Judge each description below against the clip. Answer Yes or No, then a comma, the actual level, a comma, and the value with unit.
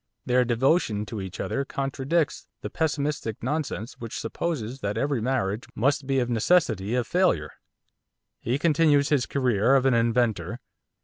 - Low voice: Yes, low, 125 Hz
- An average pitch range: Yes, average, 4.0 semitones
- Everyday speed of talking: Yes, average, 145 wpm